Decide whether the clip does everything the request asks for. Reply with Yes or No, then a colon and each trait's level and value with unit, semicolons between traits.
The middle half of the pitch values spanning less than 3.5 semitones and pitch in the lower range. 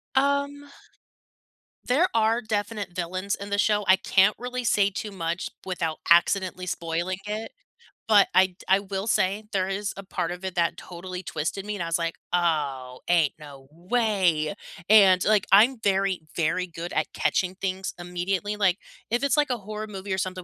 No: average, 3.1 semitones; high, 190 Hz